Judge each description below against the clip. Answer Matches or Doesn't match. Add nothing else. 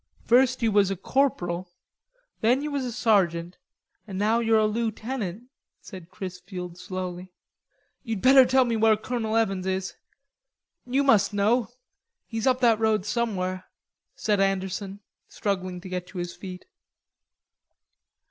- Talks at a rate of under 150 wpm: Matches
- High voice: Matches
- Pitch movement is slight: Doesn't match